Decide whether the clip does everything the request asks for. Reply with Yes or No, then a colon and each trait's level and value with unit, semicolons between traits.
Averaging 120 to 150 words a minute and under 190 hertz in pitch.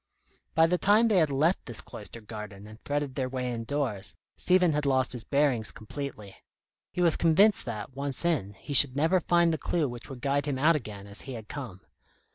No: fast, 205 wpm; medium, 140 Hz